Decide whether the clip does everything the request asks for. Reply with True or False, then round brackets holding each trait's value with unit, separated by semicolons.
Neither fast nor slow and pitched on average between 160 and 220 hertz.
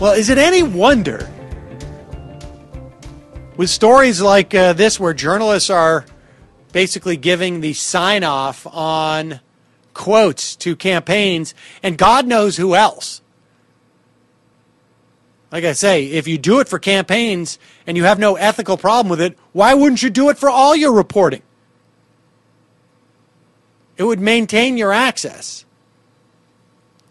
False (130 wpm; 190 Hz)